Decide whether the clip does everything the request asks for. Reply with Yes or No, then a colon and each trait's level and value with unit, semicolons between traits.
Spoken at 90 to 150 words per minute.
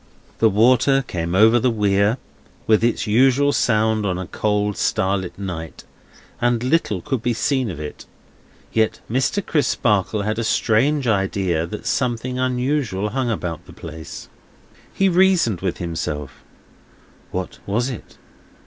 Yes: average, 140 wpm